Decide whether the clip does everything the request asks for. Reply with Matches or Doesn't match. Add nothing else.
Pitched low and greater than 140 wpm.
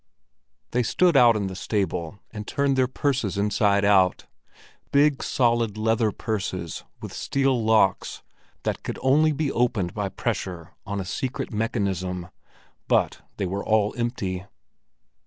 Doesn't match